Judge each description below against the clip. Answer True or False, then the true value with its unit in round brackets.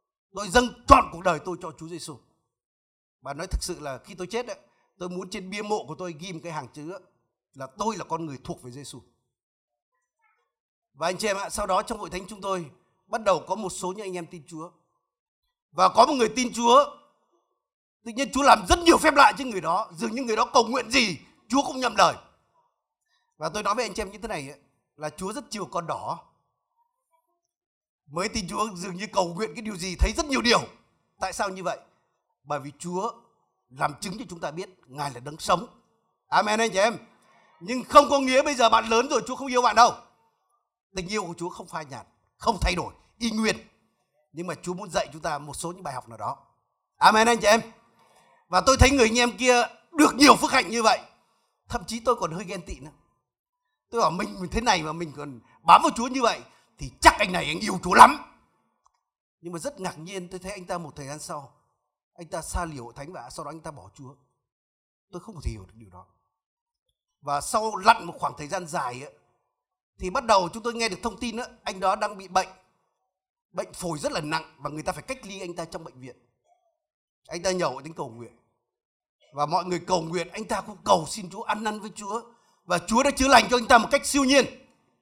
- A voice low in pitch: False (190 Hz)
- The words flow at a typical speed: True (235 wpm)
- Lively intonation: True (6.6 semitones)